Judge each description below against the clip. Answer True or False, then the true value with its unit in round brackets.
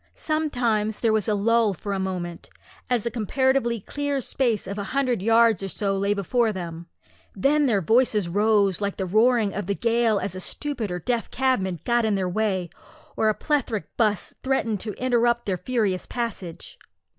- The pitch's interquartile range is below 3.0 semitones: False (3.5 semitones)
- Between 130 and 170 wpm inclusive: False (180 wpm)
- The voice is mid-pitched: False (215 Hz)